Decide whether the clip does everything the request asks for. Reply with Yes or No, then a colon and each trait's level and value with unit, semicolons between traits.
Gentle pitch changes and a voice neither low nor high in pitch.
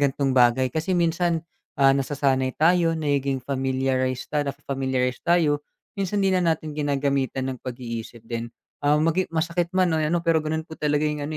No: average, 3.5 semitones; medium, 145 Hz